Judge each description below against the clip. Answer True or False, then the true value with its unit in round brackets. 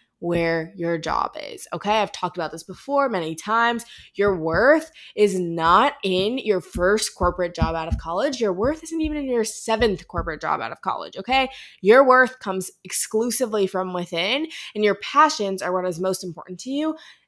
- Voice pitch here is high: True (205 Hz)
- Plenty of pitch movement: True (6.1 semitones)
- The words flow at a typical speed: True (185 wpm)